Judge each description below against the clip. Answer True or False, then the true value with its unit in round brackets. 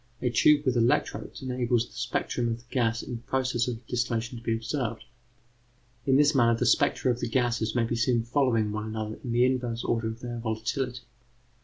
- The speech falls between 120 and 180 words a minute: False (200 wpm)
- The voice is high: False (120 Hz)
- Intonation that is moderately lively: False (1.8 semitones)